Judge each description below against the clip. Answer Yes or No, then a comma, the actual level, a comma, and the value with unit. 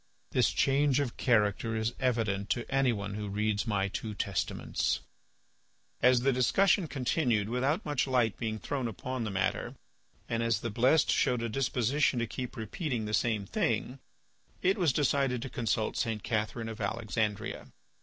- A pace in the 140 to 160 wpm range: Yes, average, 155 wpm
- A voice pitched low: Yes, low, 115 Hz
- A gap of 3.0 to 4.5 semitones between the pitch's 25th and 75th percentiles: Yes, average, 3.4 semitones